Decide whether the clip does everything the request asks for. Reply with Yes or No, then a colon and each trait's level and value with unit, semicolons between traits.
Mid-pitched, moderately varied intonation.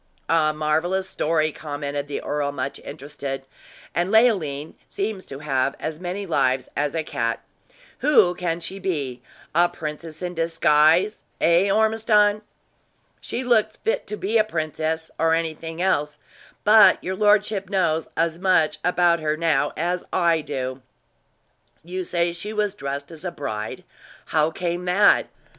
Yes: medium, 165 Hz; average, 3.9 semitones